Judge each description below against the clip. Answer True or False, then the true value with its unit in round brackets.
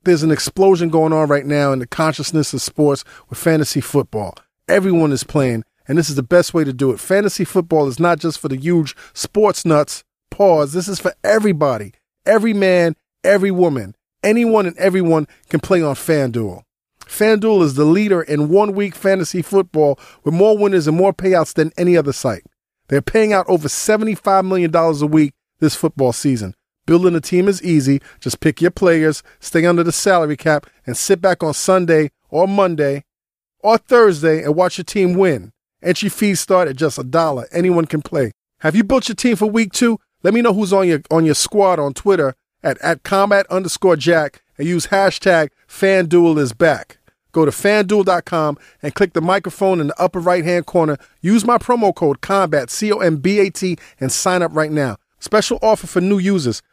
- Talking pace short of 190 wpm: False (195 wpm)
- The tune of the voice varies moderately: True (4.5 semitones)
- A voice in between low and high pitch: True (170 Hz)